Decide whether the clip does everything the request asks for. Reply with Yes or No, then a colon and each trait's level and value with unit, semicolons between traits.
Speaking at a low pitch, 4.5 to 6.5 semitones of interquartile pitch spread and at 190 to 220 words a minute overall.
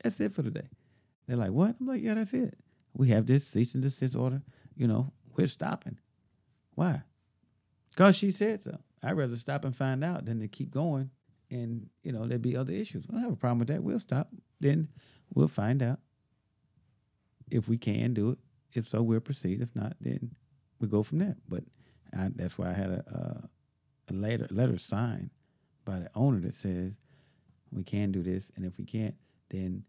Yes: low, 130 Hz; average, 4.8 semitones; fast, 205 wpm